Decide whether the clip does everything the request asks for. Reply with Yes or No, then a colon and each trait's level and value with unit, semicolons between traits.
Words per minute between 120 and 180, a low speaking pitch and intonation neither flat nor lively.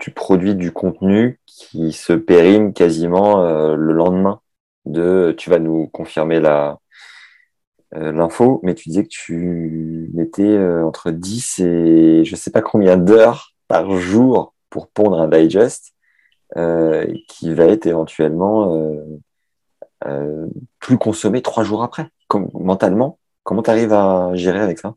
Yes: average, 150 wpm; very low, 90 Hz; average, 4.4 semitones